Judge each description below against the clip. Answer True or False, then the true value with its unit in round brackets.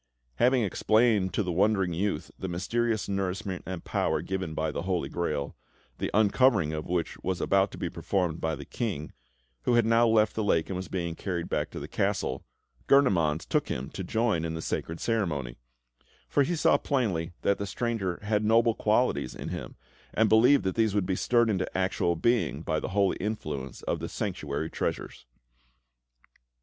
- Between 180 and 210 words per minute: True (185 wpm)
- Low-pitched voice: True (95 Hz)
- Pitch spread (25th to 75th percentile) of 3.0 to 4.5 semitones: False (4.9 semitones)